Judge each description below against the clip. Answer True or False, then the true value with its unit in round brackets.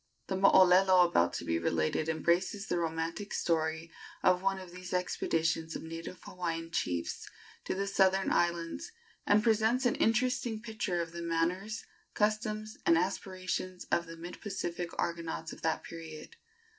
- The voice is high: False (180 Hz)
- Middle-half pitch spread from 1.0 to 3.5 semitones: True (3.1 semitones)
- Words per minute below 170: True (150 wpm)